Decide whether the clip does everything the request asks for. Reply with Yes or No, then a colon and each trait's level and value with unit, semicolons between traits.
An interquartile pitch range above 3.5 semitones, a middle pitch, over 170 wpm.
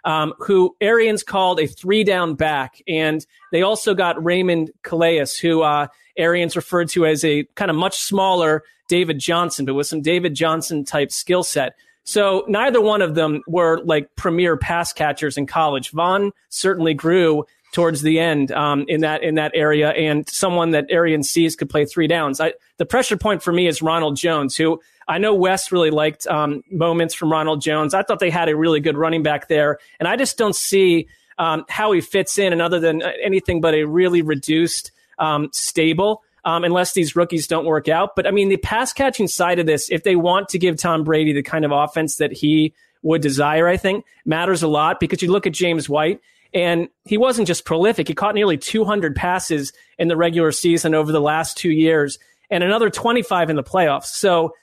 No: average, 2.8 semitones; medium, 165 Hz; fast, 205 wpm